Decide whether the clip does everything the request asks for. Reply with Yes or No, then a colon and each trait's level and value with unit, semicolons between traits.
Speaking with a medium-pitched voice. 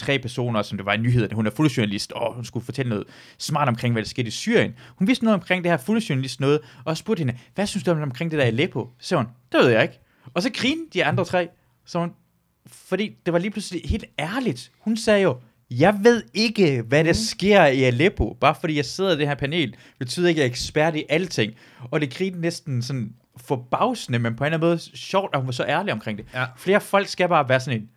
Yes: medium, 145 Hz